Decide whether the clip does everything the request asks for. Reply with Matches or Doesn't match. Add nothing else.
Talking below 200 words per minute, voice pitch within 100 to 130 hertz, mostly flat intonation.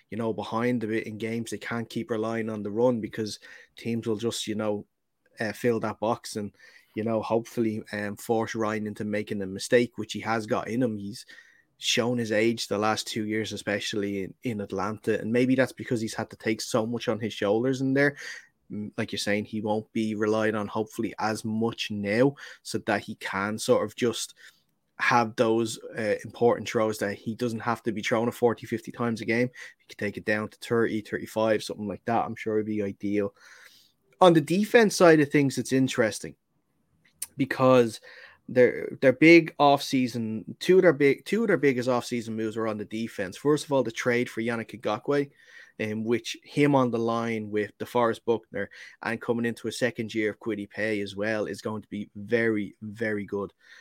Doesn't match